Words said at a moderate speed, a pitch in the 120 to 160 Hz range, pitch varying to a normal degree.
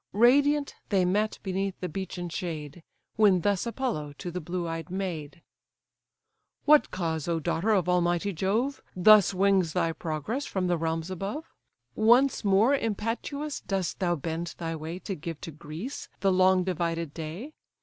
No: average, 155 wpm; medium, 185 Hz; average, 4.2 semitones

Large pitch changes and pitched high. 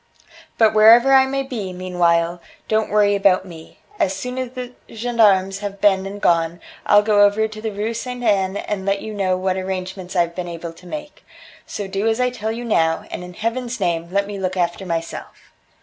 No: average, 3.3 semitones; high, 200 Hz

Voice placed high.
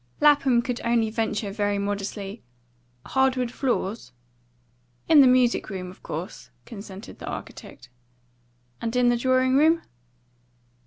Yes: high, 235 Hz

